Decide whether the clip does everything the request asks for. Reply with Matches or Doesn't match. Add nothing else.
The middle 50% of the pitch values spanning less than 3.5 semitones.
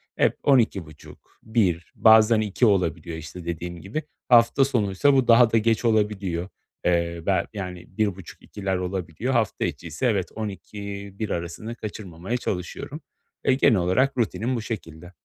Doesn't match